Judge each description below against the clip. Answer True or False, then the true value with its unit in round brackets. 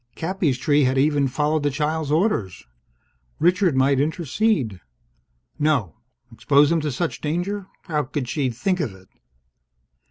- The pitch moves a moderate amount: True (3.9 semitones)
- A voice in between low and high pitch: True (150 Hz)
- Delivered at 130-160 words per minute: True (135 wpm)